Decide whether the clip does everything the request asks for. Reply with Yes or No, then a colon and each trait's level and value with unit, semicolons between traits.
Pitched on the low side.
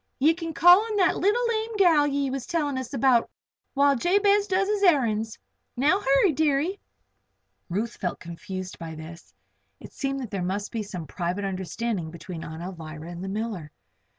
No: very high, 255 Hz